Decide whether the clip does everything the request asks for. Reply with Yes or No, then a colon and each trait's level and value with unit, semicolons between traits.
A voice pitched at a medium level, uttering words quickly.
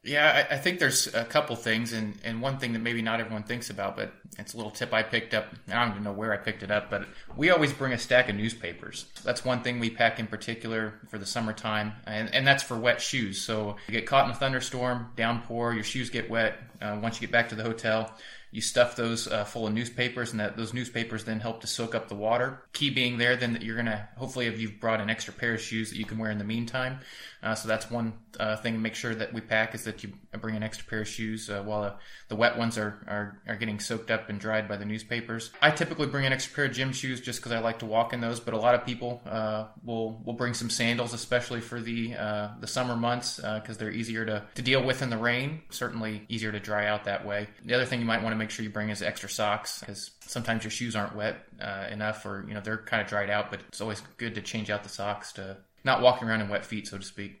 No: low, 115 Hz; fast, 270 wpm